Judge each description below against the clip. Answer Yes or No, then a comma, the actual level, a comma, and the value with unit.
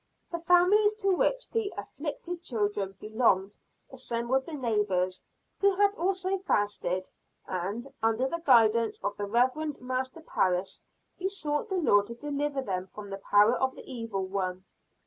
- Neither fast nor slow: Yes, average, 145 wpm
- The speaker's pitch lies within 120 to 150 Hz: No, high, 245 Hz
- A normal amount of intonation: No, wide, 8.6 semitones